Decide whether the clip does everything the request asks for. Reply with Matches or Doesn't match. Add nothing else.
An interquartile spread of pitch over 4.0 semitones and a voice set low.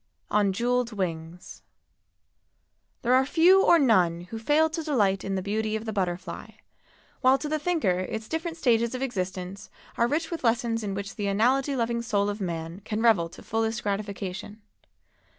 Doesn't match